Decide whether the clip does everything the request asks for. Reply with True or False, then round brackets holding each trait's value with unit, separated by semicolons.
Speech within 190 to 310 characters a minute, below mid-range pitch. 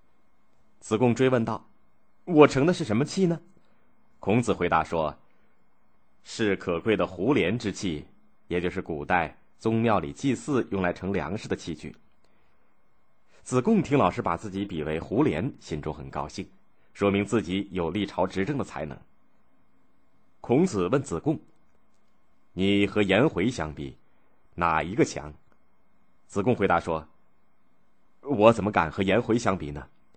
True (205 characters per minute; 95 Hz)